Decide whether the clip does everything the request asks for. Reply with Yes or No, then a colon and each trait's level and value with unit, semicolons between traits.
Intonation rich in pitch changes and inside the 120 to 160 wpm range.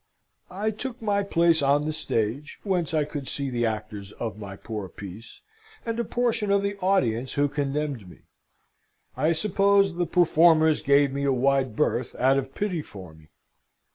No: wide, 7.4 semitones; average, 170 wpm